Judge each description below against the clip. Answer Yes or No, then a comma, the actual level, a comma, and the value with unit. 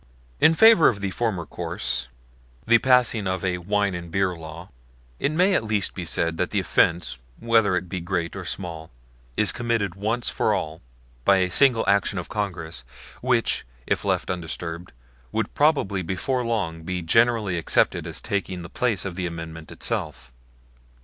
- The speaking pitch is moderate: No, very low, 95 Hz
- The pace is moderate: Yes, average, 170 wpm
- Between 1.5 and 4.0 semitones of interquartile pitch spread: No, average, 4.9 semitones